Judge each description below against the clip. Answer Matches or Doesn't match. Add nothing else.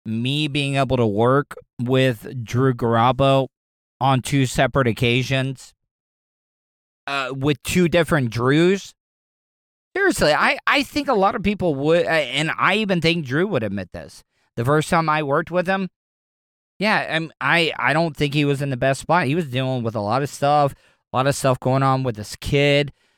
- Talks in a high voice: Doesn't match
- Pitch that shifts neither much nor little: Matches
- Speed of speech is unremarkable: Matches